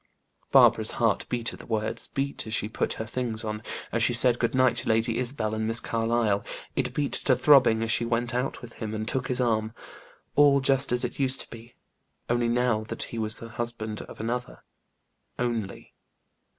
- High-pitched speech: No, low, 120 Hz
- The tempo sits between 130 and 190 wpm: No, average, 200 wpm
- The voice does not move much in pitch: Yes, narrow, 2.0 semitones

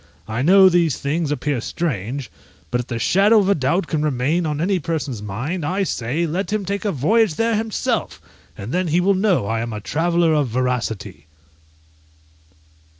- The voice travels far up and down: Yes, wide, 6.7 semitones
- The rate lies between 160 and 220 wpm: Yes, average, 180 wpm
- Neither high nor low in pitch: Yes, medium, 160 Hz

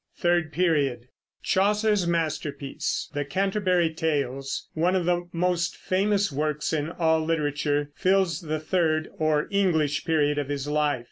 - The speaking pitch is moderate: Yes, medium, 160 Hz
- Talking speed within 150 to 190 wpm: No, slow, 135 wpm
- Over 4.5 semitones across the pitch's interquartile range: No, average, 3.4 semitones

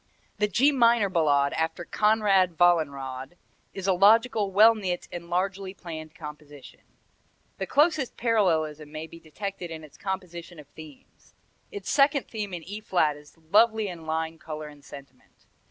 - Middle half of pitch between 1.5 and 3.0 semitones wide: No, average, 5.1 semitones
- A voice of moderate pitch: Yes, medium, 175 Hz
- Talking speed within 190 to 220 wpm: No, average, 155 wpm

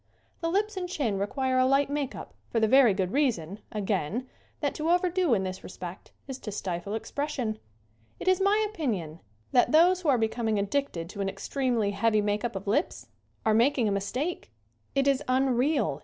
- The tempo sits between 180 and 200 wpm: Yes, average, 190 wpm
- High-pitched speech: Yes, high, 245 Hz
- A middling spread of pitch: No, wide, 6.2 semitones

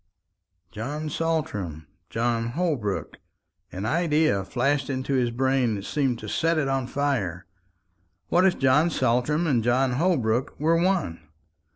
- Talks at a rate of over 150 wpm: No, slow, 135 wpm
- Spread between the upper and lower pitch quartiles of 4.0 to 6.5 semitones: Yes, average, 4.9 semitones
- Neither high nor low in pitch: No, low, 130 Hz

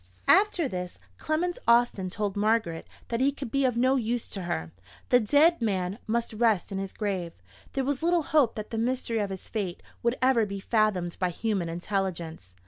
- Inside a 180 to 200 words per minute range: Yes, average, 190 wpm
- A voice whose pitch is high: Yes, high, 220 Hz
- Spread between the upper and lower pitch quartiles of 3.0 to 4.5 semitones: No, average, 5.0 semitones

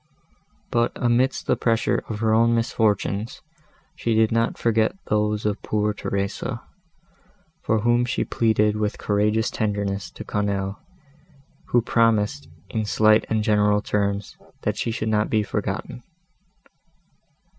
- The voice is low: Yes, low, 110 Hz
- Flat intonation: Yes, narrow, 1.8 semitones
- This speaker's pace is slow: Yes, slow, 130 wpm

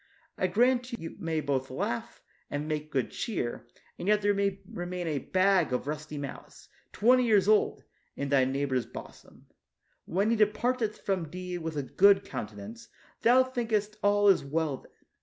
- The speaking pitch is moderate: Yes, medium, 180 Hz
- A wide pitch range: Yes, wide, 6.7 semitones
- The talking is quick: No, average, 165 wpm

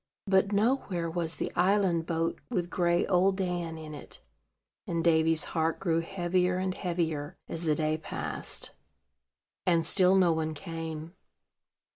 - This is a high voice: No, medium, 170 Hz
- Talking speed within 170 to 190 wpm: No, average, 140 wpm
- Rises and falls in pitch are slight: Yes, narrow, 2.2 semitones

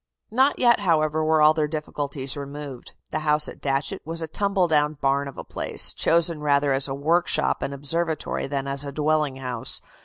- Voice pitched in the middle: Yes, medium, 150 Hz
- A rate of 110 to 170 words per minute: No, average, 190 wpm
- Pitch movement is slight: Yes, narrow, 2.3 semitones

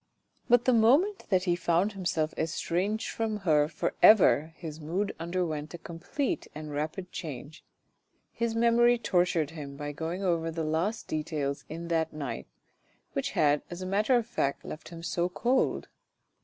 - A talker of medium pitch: Yes, medium, 170 Hz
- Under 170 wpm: Yes, average, 160 wpm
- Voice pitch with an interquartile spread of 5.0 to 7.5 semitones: Yes, average, 5.3 semitones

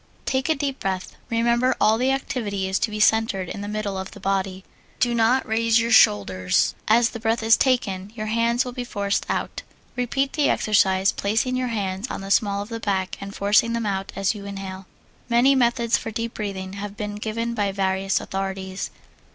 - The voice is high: Yes, high, 215 Hz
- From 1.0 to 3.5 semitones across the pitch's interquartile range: Yes, average, 3.2 semitones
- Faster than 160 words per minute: Yes, average, 200 wpm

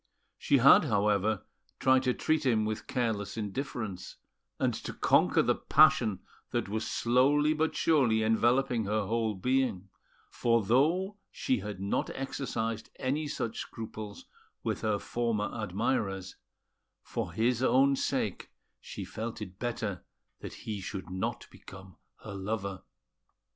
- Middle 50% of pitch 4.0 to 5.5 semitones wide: Yes, average, 4.3 semitones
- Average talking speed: No, slow, 130 wpm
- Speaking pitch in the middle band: No, low, 115 Hz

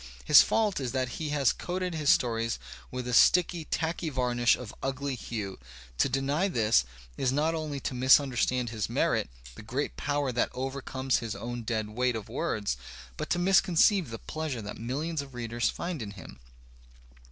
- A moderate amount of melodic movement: Yes, average, 4.5 semitones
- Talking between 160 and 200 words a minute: Yes, average, 175 wpm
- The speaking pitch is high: No, low, 130 Hz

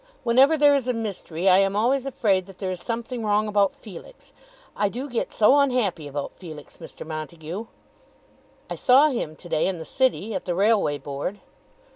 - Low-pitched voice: No, high, 205 Hz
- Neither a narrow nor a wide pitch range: No, wide, 6.1 semitones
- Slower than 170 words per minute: No, average, 185 wpm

